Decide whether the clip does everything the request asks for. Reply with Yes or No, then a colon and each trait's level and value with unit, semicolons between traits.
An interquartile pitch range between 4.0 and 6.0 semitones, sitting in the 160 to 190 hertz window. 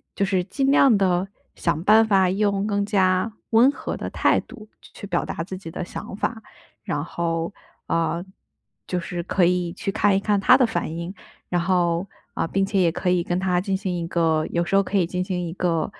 No: narrow, 2.6 semitones; medium, 185 Hz